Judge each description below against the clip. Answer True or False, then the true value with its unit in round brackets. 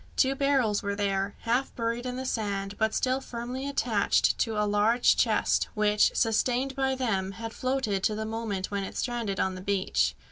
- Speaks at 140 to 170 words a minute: False (185 wpm)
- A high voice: True (225 Hz)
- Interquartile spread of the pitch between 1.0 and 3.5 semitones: False (3.9 semitones)